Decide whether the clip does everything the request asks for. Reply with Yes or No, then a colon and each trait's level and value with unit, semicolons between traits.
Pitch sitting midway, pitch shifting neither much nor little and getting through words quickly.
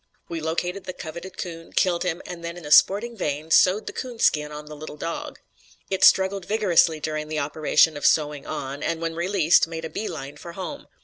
Yes: medium, 165 Hz; average, 3.2 semitones; fast, 210 wpm